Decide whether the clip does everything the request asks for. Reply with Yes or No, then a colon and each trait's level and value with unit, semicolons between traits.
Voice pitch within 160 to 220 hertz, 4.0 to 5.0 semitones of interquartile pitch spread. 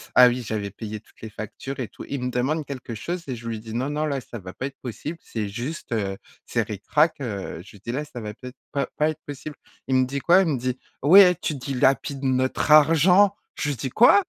No: low, 130 Hz; average, 4.7 semitones